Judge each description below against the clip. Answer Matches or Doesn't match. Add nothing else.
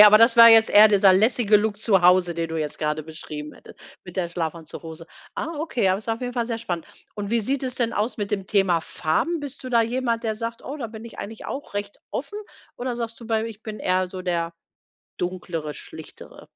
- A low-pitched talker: Doesn't match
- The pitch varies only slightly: Doesn't match